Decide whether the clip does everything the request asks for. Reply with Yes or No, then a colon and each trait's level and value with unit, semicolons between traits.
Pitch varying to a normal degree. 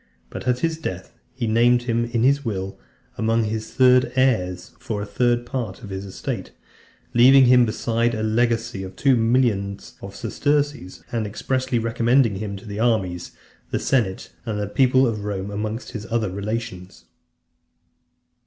Yes: average, 3.3 semitones